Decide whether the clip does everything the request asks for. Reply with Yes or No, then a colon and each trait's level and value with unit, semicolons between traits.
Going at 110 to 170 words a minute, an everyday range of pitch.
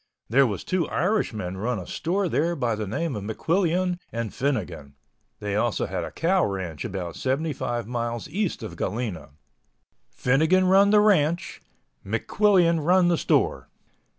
No: average, 150 wpm; wide, 8.9 semitones